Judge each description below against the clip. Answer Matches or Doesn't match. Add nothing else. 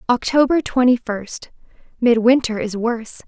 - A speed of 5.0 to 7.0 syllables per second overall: Doesn't match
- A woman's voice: Matches